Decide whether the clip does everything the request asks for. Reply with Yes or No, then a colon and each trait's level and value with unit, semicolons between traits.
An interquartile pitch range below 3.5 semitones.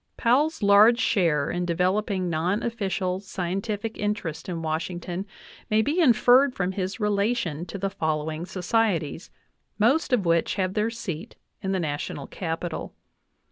No: average, 4.3 semitones